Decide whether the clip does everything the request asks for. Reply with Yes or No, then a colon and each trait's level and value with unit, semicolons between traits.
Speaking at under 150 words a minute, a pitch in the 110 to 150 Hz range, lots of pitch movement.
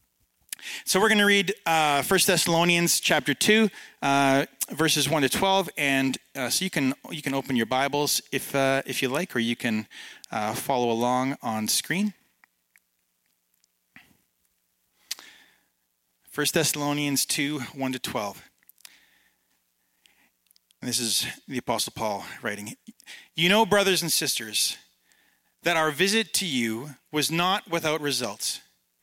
Yes: slow, 135 wpm; medium, 140 Hz; wide, 6.3 semitones